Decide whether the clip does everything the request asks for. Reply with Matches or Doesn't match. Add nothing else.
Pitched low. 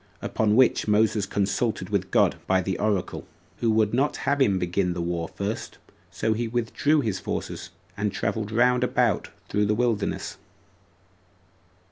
Matches